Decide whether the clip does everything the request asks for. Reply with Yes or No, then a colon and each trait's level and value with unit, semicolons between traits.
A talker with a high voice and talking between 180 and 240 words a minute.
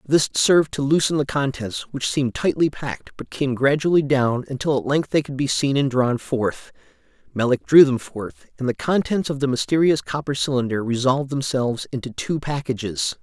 No: low, 135 Hz; average, 185 wpm